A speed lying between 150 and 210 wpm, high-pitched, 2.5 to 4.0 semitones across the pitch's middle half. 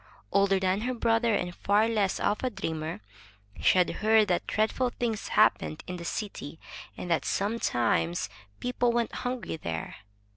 No: average, 155 wpm; high, 205 Hz; average, 4.6 semitones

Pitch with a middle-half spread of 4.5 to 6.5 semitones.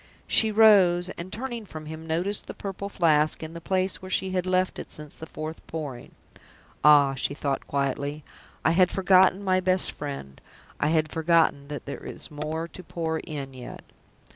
No: average, 3.9 semitones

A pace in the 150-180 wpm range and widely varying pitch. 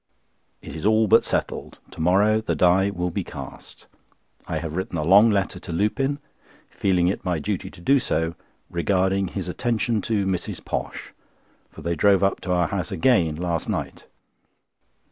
No: average, 165 wpm; average, 3.3 semitones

